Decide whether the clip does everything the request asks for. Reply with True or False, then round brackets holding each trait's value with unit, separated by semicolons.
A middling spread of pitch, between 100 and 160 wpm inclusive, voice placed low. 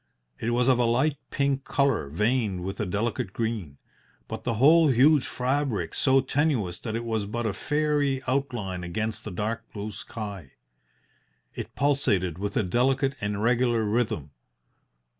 True (4.7 semitones; 155 wpm; 115 Hz)